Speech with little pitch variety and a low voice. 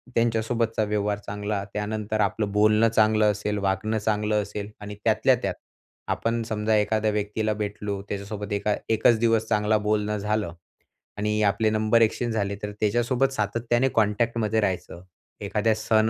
Yes: narrow, 1.2 semitones; low, 105 Hz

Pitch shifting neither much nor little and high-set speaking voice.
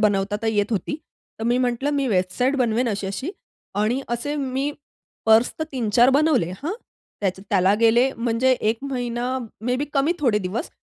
Yes: average, 3.9 semitones; high, 240 Hz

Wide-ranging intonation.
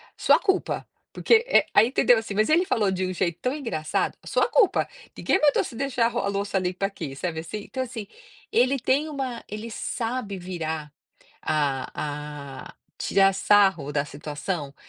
Yes: wide, 7.6 semitones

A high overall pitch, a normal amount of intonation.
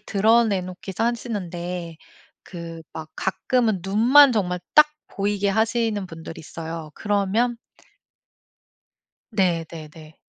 Yes: high, 195 Hz; average, 4.7 semitones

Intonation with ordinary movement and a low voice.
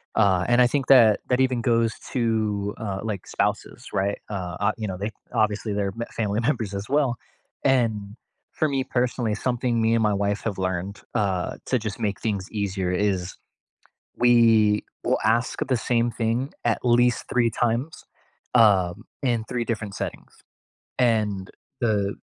Yes: average, 3.0 semitones; low, 110 Hz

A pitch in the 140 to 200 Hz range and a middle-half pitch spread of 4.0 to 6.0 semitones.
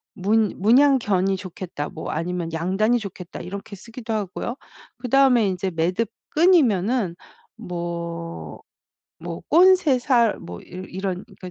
Yes: high, 195 Hz; average, 5.1 semitones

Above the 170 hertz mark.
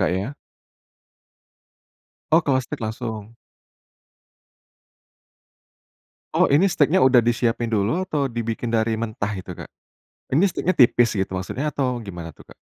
No: low, 120 Hz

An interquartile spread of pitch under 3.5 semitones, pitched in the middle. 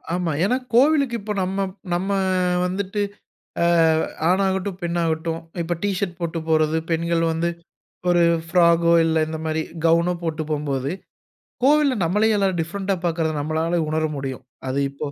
Yes: average, 3.1 semitones; medium, 170 Hz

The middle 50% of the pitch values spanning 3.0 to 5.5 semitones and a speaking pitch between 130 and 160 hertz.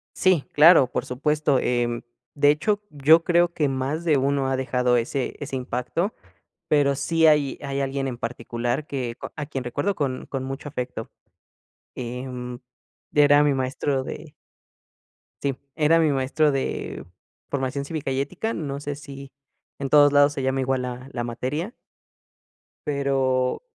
No: narrow, 2.5 semitones; medium, 140 Hz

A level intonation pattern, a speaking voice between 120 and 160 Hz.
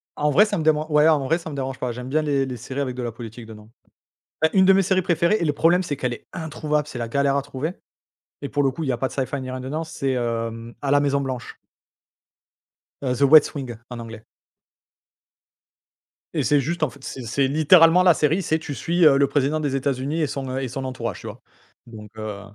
No: average, 3.6 semitones; medium, 140 Hz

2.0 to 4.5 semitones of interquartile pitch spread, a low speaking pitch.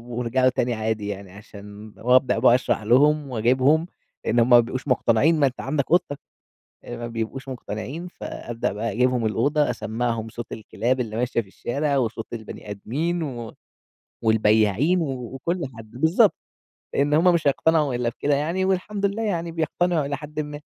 No: average, 5.1 semitones; low, 130 Hz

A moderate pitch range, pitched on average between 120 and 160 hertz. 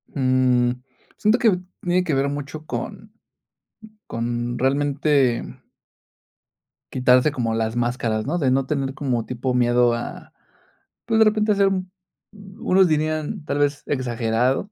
Yes: average, 4.3 semitones; low, 135 Hz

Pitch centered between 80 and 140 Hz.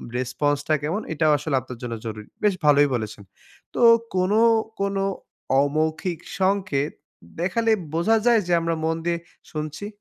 No: medium, 160 Hz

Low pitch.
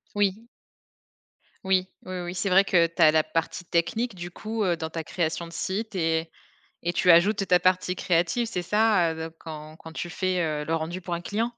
No: medium, 175 Hz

